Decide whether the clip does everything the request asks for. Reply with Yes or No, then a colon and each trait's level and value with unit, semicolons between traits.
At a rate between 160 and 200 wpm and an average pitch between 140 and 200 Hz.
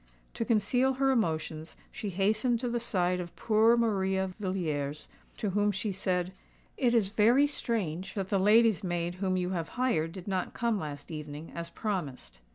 Yes: average, 170 wpm; high, 190 Hz